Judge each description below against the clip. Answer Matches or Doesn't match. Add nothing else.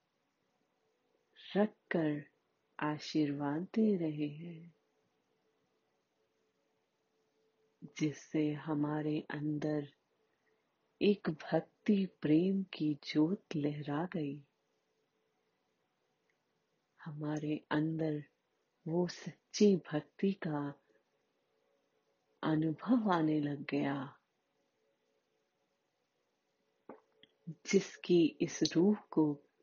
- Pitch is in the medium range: Matches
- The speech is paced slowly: Matches